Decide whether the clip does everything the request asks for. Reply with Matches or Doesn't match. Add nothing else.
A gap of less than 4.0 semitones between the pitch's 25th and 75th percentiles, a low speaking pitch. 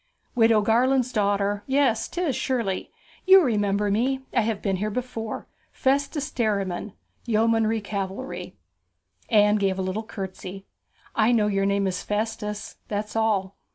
Doesn't match